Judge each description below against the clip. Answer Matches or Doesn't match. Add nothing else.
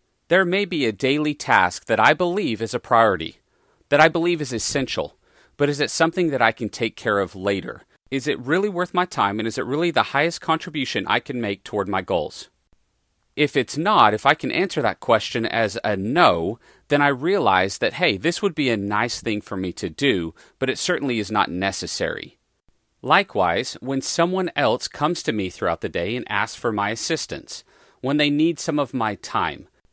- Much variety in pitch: Matches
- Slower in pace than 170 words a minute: Doesn't match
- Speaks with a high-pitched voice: Doesn't match